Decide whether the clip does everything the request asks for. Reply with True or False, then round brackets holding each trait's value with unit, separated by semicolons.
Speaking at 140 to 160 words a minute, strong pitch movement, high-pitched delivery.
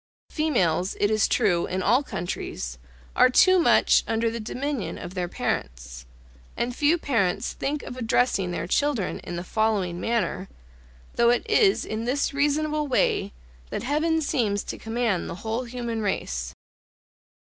True (150 wpm; 7.2 semitones; 230 Hz)